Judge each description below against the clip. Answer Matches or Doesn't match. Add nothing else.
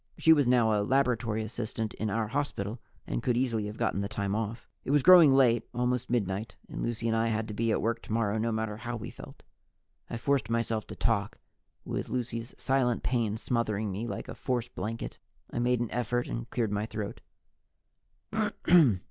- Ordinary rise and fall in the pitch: Doesn't match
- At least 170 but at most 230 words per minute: Matches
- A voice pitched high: Doesn't match